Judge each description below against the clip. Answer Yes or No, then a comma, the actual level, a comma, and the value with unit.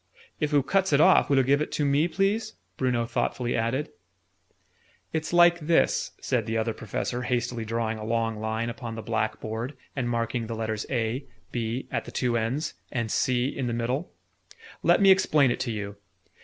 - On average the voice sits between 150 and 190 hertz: No, low, 120 Hz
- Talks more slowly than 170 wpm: No, average, 190 wpm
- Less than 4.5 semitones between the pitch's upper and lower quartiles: Yes, average, 4.0 semitones